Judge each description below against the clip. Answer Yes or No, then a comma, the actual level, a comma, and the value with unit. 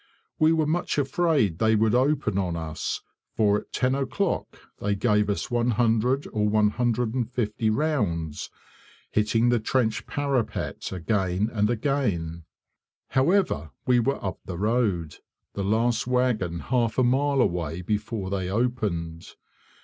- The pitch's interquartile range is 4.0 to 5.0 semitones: Yes, average, 4.5 semitones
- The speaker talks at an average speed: No, slow, 130 wpm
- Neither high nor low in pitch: No, low, 110 Hz